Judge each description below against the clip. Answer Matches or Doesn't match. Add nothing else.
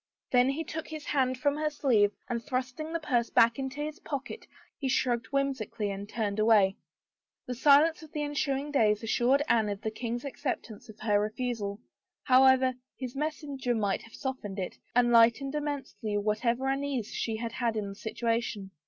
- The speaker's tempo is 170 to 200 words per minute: Matches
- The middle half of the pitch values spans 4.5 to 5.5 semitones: Doesn't match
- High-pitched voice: Matches